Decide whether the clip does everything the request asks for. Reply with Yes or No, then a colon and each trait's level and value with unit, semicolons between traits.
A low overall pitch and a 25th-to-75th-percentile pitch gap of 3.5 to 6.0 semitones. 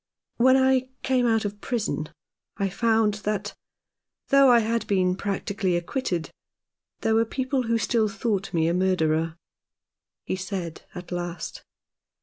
No: high, 205 Hz; average, 4.2 semitones